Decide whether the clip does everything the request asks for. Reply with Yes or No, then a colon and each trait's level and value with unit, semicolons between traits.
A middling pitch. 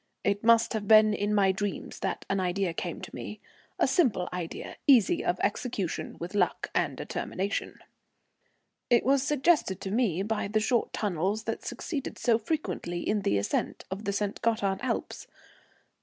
No: high, 205 Hz